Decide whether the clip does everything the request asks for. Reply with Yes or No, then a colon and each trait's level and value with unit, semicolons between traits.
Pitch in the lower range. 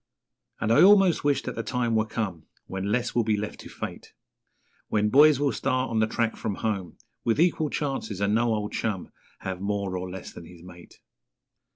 Yes: low, 110 Hz